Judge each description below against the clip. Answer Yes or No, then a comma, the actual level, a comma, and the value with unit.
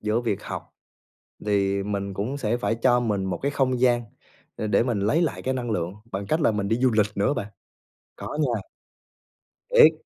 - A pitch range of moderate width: Yes, average, 4.2 semitones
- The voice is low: Yes, low, 115 Hz